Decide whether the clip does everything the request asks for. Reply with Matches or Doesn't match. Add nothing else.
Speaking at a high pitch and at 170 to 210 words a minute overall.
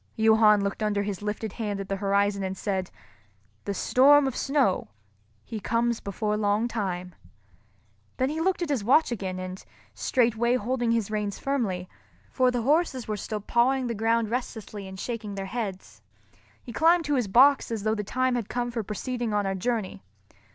Matches